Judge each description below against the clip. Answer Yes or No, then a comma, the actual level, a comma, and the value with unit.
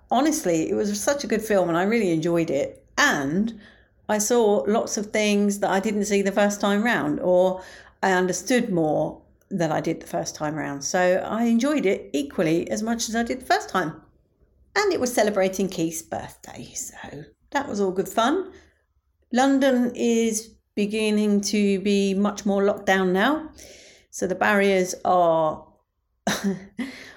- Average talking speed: Yes, average, 170 wpm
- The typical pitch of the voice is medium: No, high, 205 Hz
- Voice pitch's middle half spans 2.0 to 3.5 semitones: No, average, 3.9 semitones